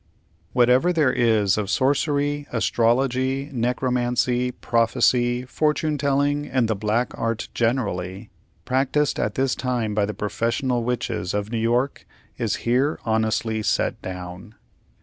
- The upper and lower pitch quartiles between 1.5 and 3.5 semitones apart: Yes, average, 3.1 semitones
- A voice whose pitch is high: No, low, 120 Hz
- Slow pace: Yes, slow, 125 wpm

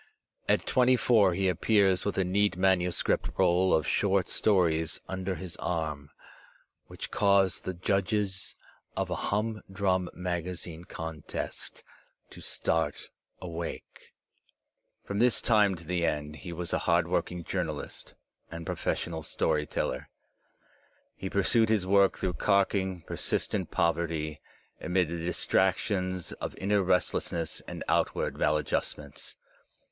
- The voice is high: No, very low, 90 Hz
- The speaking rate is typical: No, slow, 125 wpm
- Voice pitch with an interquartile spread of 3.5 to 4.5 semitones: No, average, 2.7 semitones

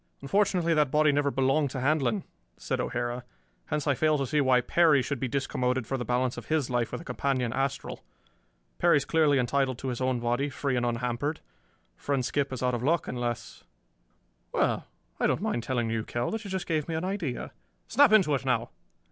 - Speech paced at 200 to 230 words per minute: Yes, fast, 205 wpm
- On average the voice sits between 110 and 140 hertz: Yes, low, 135 Hz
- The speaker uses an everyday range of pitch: Yes, average, 3.6 semitones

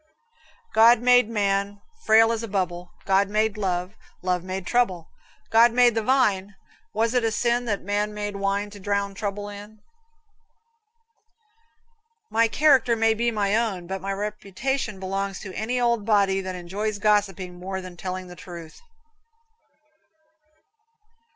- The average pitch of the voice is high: Yes, high, 205 Hz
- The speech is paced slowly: No, average, 145 wpm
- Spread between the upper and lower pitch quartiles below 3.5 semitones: Yes, average, 2.7 semitones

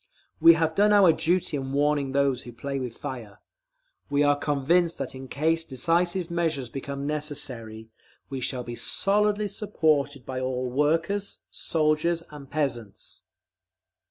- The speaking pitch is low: No, medium, 145 Hz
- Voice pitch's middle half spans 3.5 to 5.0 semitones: Yes, average, 4.0 semitones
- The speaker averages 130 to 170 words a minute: Yes, average, 140 wpm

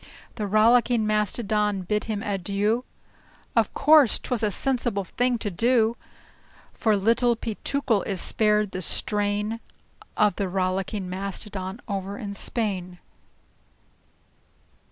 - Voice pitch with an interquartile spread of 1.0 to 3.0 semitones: Yes, average, 2.7 semitones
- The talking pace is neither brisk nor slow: No, slow, 115 wpm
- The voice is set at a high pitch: Yes, high, 210 Hz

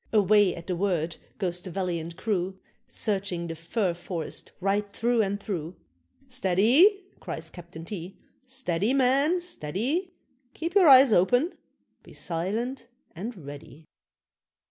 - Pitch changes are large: Yes, wide, 6.3 semitones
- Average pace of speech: No, slow, 125 wpm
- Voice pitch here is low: No, high, 200 Hz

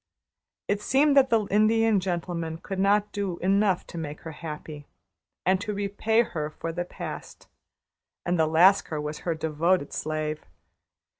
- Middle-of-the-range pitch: Yes, medium, 180 Hz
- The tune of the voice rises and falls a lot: No, average, 4.3 semitones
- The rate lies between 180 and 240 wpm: No, average, 150 wpm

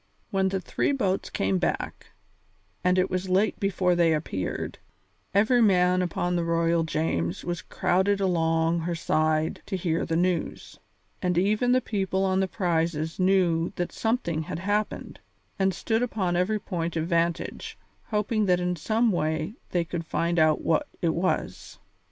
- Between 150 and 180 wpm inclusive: Yes, average, 160 wpm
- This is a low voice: No, medium, 180 Hz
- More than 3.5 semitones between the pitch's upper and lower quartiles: No, average, 2.7 semitones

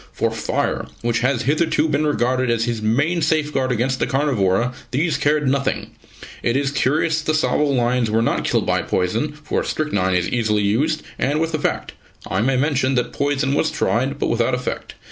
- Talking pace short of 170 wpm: No, average, 185 wpm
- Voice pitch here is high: No, low, 135 Hz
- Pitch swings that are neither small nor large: Yes, average, 4.1 semitones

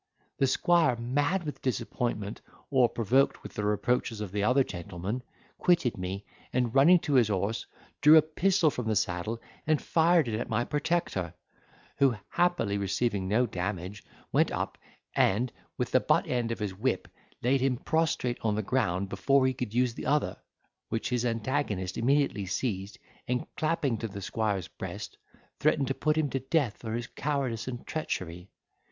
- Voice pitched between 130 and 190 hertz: No, low, 120 Hz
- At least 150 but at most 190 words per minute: Yes, average, 170 wpm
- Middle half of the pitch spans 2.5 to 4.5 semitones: No, average, 5.1 semitones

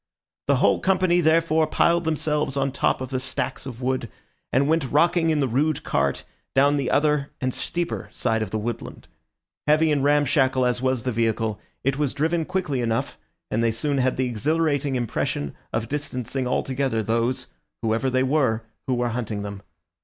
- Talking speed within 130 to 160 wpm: No, average, 175 wpm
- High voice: No, low, 135 Hz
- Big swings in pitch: No, average, 3.9 semitones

